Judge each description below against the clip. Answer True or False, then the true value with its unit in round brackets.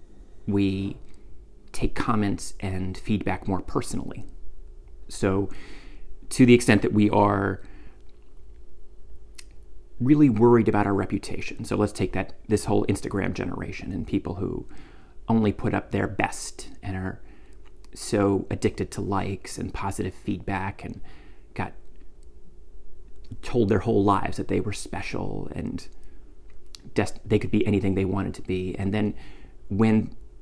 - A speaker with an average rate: False (130 wpm)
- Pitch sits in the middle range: False (95 Hz)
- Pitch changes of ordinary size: False (6.7 semitones)